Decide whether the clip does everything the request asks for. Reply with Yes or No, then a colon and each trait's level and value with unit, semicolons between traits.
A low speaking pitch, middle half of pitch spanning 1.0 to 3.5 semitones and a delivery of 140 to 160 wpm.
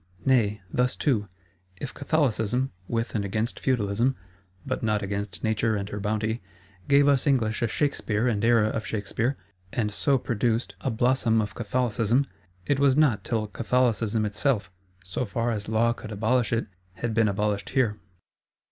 Yes: low, 115 Hz; average, 3.1 semitones; average, 155 wpm